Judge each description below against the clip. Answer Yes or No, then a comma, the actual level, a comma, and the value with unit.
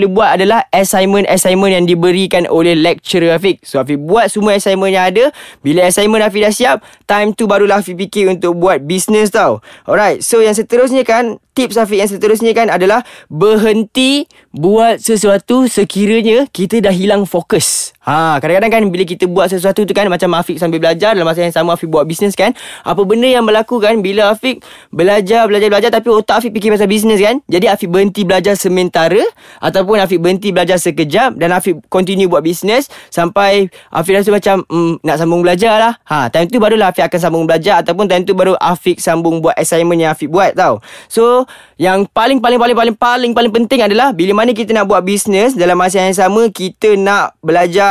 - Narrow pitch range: No, average, 3.5 semitones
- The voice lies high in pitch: Yes, high, 200 Hz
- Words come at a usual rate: No, fast, 195 wpm